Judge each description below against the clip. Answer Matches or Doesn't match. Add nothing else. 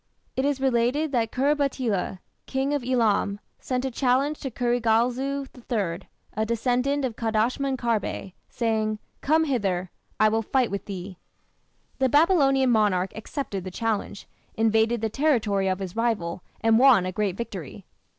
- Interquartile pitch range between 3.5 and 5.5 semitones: Matches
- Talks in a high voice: Matches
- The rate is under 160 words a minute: Matches